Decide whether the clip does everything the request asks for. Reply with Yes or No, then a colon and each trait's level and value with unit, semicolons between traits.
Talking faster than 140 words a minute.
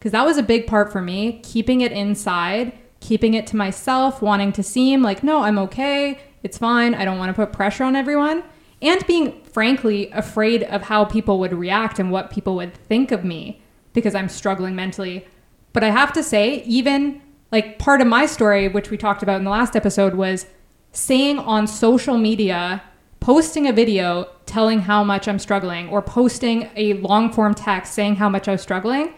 Yes: average, 195 wpm